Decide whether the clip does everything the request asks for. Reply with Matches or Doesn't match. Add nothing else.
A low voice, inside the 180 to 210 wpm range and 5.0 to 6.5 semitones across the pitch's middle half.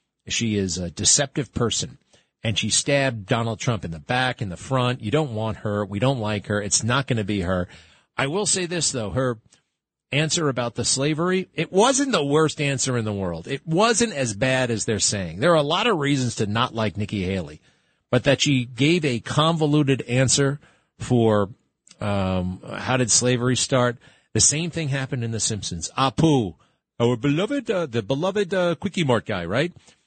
Matches